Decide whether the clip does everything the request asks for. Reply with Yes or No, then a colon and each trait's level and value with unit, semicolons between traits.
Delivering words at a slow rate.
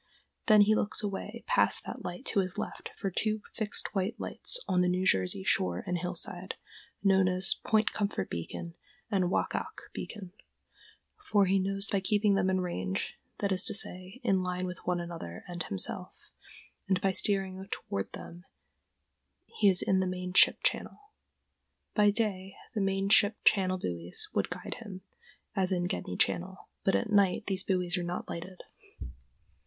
No: average, 170 wpm